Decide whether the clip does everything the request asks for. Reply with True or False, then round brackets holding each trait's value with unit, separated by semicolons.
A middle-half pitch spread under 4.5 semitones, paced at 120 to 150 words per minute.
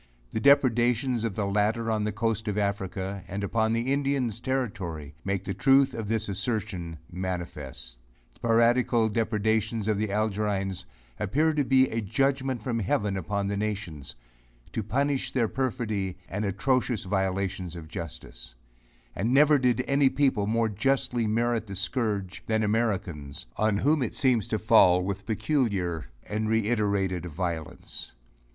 True (3.6 semitones; 145 wpm)